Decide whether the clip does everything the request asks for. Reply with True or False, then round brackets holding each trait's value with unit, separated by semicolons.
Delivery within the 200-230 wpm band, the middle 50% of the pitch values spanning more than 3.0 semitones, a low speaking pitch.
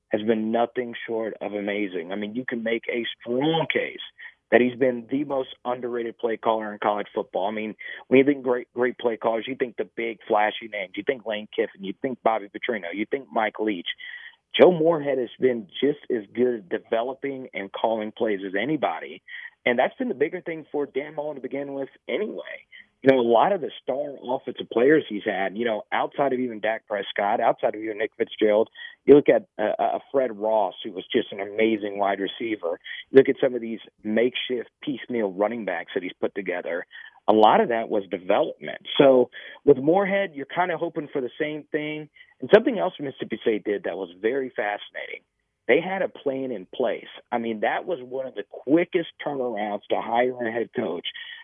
True (205 wpm; 5.3 semitones; 125 Hz)